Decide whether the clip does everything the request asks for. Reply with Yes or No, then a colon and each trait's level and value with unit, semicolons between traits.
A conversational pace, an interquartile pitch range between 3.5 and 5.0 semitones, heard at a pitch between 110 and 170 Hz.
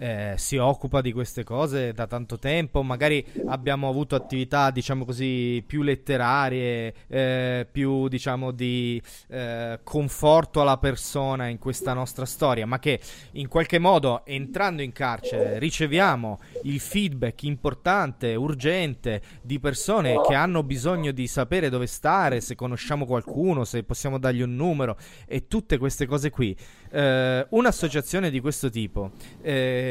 No: average, 140 wpm; average, 3.1 semitones; low, 135 Hz